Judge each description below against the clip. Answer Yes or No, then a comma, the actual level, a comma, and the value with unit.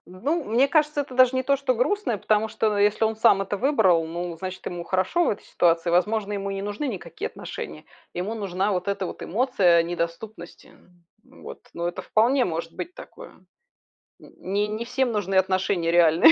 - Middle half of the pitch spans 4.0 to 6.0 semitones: Yes, average, 5.3 semitones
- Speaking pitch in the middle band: No, high, 200 Hz